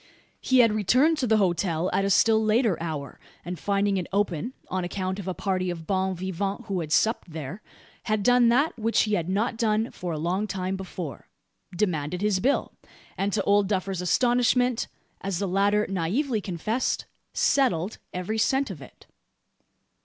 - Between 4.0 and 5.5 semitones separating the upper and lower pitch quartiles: No, average, 3.6 semitones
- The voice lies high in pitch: Yes, high, 195 Hz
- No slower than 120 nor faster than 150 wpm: No, average, 175 wpm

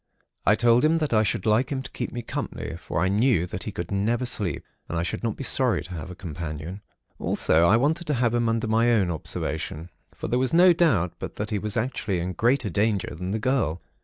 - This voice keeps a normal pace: No, fast, 240 wpm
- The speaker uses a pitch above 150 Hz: No, low, 110 Hz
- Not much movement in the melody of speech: No, average, 5.3 semitones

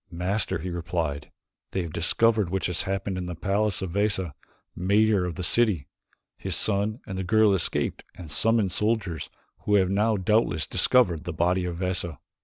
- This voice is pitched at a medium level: No, very low, 95 Hz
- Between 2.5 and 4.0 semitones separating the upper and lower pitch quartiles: Yes, average, 3.4 semitones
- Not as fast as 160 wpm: No, average, 180 wpm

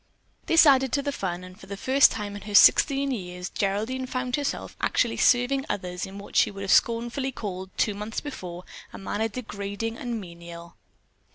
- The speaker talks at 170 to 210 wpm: Yes, average, 185 wpm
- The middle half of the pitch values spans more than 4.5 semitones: Yes, average, 5.2 semitones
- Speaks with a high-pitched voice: Yes, high, 210 Hz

